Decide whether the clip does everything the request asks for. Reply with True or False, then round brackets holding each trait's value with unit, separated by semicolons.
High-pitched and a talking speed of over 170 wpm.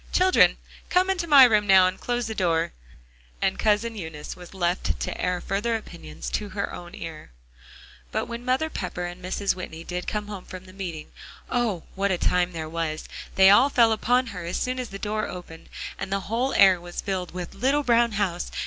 True (195 Hz; 205 wpm)